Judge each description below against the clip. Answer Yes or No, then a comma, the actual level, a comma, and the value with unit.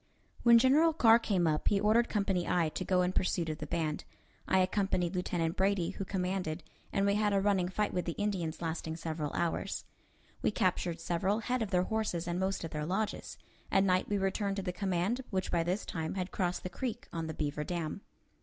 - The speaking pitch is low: No, medium, 185 Hz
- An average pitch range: Yes, average, 3.1 semitones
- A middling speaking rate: No, fast, 210 wpm